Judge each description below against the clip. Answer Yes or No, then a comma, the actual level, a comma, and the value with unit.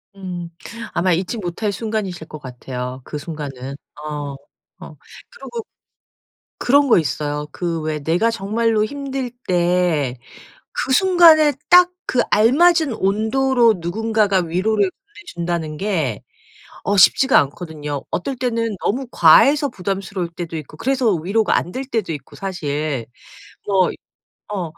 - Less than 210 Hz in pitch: Yes, high, 190 Hz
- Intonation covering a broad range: Yes, wide, 6.3 semitones